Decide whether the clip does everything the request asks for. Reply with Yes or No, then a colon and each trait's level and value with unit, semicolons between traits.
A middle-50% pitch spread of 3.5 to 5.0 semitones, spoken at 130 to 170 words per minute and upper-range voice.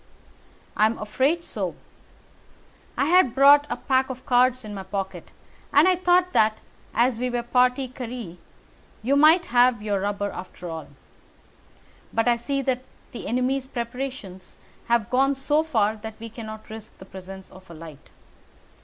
Yes: average, 4.2 semitones; average, 160 wpm; high, 240 Hz